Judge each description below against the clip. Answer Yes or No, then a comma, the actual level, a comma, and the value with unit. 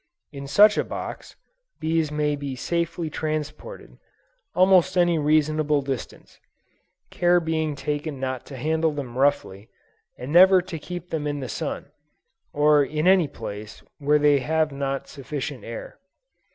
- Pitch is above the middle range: No, medium, 150 Hz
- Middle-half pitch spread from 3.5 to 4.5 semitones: No, average, 2.7 semitones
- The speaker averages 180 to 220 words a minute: No, average, 140 wpm